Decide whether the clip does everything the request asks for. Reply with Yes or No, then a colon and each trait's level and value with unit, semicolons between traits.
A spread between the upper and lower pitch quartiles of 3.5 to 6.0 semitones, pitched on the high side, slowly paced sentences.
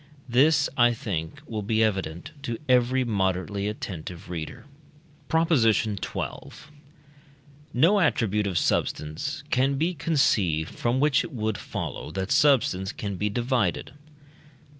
No: wide, 5.6 semitones; low, 110 Hz; slow, 120 wpm